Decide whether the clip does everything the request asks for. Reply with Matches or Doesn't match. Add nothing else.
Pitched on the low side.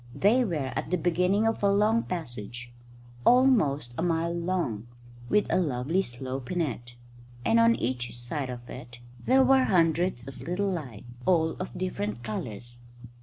Doesn't match